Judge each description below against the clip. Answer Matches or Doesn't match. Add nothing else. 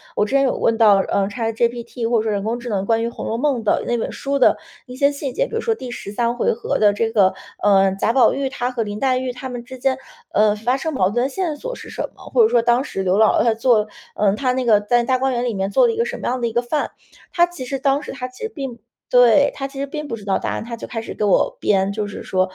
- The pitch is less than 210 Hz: Doesn't match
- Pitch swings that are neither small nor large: Matches